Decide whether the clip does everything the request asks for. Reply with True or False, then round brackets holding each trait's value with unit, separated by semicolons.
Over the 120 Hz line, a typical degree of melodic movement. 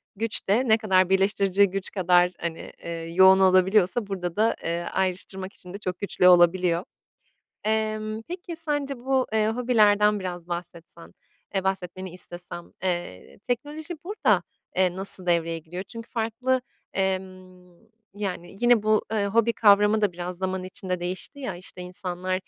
True (190 Hz; 3.2 semitones)